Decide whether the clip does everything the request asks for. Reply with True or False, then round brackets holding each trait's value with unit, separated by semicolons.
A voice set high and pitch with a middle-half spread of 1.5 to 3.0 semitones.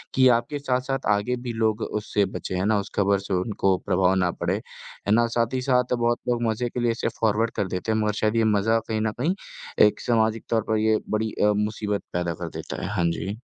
False (110 Hz; 2.6 semitones)